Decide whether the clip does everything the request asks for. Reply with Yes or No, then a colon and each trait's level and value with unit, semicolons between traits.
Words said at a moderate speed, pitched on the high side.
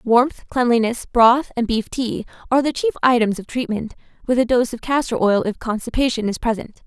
Yes: average, 190 wpm; high, 240 Hz